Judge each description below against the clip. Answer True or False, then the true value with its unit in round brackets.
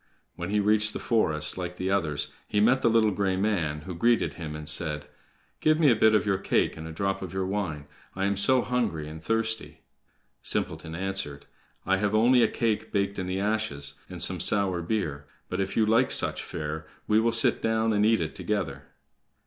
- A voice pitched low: True (100 Hz)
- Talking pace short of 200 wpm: False (205 wpm)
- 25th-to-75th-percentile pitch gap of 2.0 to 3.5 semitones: False (5.1 semitones)